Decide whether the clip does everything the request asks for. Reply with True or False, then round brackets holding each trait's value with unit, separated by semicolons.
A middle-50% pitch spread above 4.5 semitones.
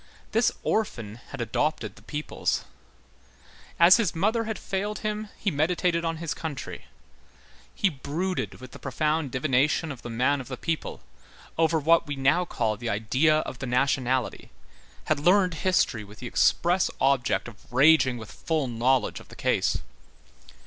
True (4.9 semitones)